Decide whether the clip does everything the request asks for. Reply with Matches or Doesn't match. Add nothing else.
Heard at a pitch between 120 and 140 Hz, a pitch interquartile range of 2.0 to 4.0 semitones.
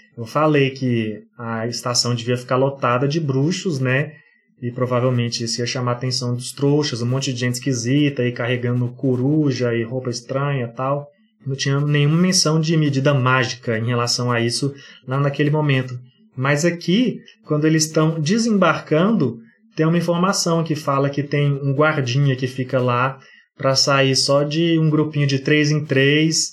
Matches